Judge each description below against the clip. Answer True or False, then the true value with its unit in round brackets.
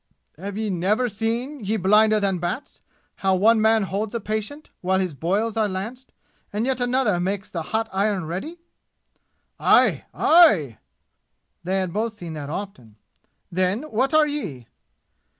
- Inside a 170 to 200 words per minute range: False (150 wpm)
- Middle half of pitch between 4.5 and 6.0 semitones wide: False (3.6 semitones)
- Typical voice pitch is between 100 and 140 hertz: False (205 Hz)